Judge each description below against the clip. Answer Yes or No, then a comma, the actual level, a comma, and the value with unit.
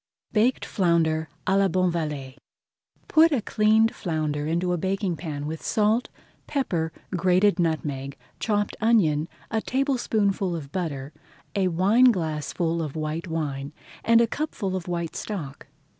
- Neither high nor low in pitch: Yes, medium, 175 Hz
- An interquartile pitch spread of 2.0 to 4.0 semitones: No, average, 5.0 semitones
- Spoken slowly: Yes, slow, 130 wpm